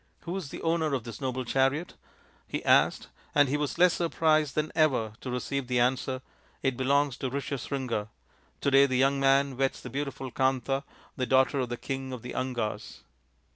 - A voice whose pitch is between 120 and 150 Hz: Yes, low, 135 Hz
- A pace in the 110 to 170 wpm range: No, average, 195 wpm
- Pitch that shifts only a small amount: Yes, narrow, 1.8 semitones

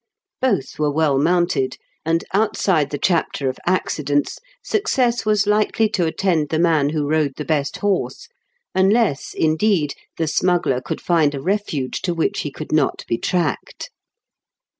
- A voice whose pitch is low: No, medium, 165 Hz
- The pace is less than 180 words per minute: Yes, average, 150 wpm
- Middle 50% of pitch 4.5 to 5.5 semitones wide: Yes, average, 5.0 semitones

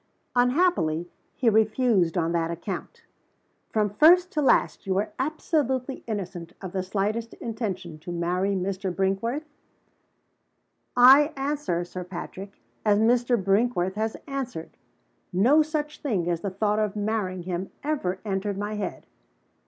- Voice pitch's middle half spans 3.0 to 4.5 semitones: No, average, 5.2 semitones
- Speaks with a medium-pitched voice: No, high, 205 Hz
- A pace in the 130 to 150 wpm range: Yes, slow, 135 wpm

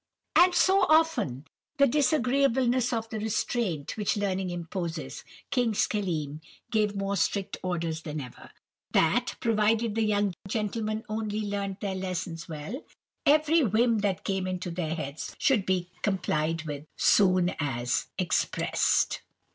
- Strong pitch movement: No, average, 4.9 semitones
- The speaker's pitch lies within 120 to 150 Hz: No, high, 200 Hz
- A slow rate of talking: Yes, slow, 130 wpm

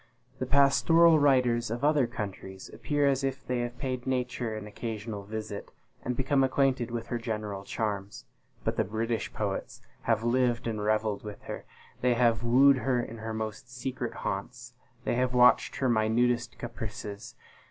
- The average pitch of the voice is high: No, low, 120 Hz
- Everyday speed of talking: Yes, average, 165 wpm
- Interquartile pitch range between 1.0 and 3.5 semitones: Yes, average, 2.7 semitones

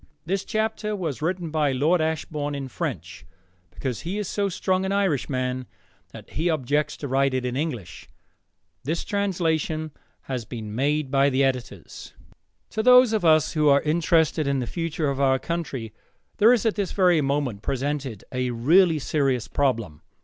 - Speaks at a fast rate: No, average, 165 wpm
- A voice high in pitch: No, medium, 150 Hz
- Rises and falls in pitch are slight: No, average, 4.7 semitones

